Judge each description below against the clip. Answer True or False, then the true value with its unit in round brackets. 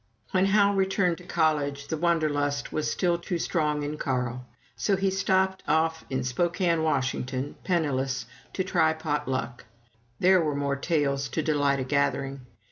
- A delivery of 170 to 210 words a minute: False (155 wpm)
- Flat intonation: False (4.0 semitones)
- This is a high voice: False (155 Hz)